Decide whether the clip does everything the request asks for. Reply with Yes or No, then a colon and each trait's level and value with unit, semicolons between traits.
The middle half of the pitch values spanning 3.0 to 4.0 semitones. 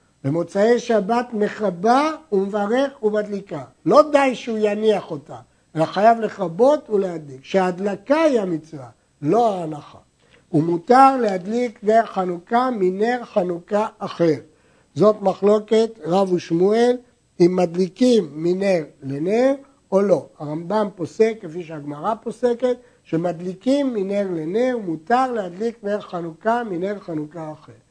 No: average, 5.2 semitones